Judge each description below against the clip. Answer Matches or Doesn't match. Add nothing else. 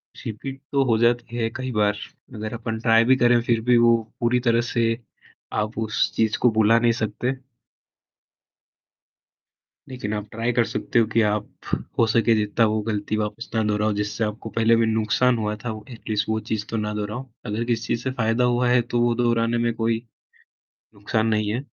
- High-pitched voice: Doesn't match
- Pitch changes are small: Matches